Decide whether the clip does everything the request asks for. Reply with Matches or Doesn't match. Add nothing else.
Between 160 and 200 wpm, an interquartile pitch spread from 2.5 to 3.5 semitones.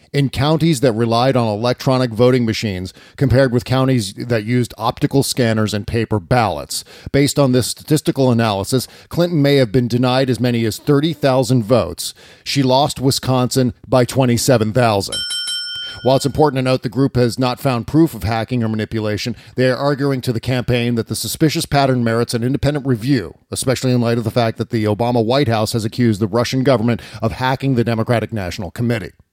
Matches